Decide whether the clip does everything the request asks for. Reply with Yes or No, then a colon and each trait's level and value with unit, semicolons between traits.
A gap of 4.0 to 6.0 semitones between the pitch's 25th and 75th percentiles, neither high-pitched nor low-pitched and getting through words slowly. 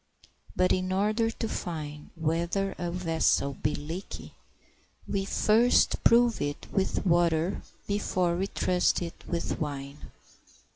No: average, 3.4 semitones; medium, 175 Hz; slow, 125 wpm